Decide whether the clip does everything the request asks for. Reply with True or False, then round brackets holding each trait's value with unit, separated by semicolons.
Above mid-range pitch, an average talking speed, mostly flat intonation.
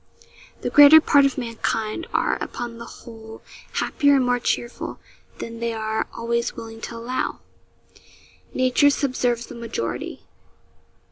False (235 Hz; 130 wpm; 2.0 semitones)